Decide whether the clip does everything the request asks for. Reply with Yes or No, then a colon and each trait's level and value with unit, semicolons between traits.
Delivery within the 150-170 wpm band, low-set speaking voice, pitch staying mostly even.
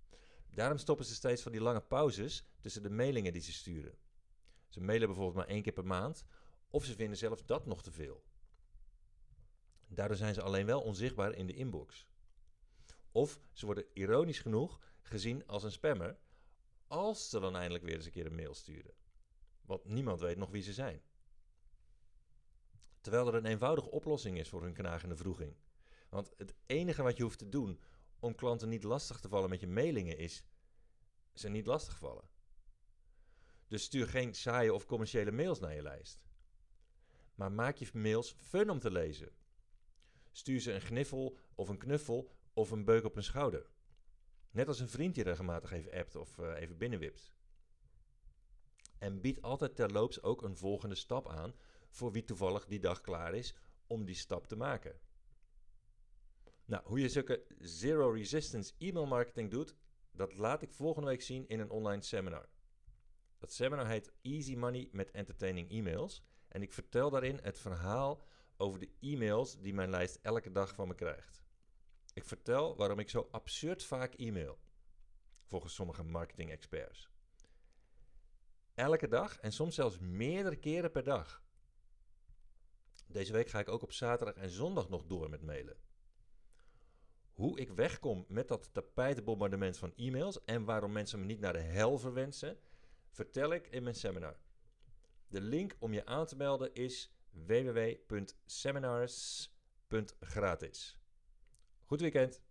No: average, 160 wpm; low, 105 Hz; average, 5.0 semitones